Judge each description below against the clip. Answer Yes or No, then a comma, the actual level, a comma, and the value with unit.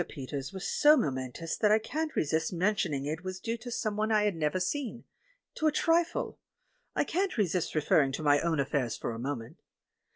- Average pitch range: No, wide, 7.9 semitones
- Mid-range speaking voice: Yes, medium, 180 Hz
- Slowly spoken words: No, average, 200 wpm